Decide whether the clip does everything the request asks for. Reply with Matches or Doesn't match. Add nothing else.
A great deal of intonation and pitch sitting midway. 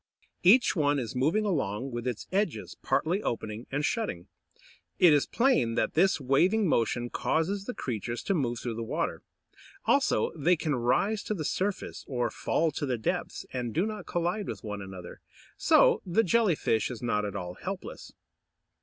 Matches